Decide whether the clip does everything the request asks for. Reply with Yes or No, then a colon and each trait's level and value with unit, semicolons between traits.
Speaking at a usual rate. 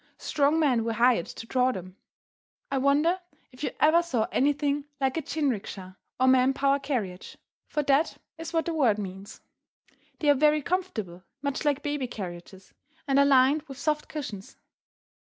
Yes: average, 170 wpm